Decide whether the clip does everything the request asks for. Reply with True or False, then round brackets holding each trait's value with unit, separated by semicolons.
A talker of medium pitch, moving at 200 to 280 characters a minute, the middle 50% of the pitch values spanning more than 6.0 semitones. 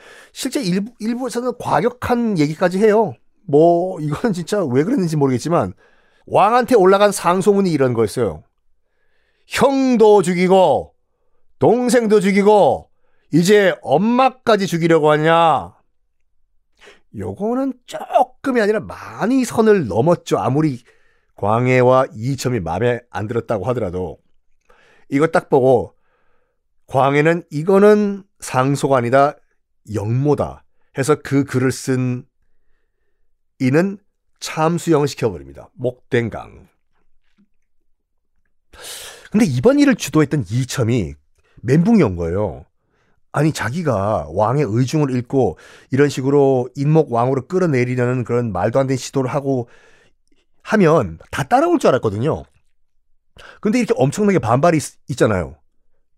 True (155 Hz; 255 characters per minute; 8.9 semitones)